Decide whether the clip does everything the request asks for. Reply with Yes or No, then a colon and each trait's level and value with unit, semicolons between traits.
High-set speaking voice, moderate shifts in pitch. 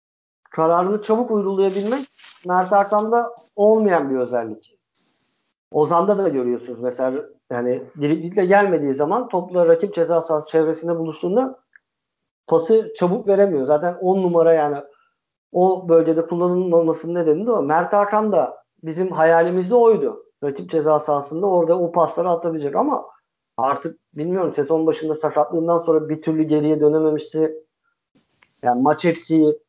No: medium, 165 Hz; average, 4.3 semitones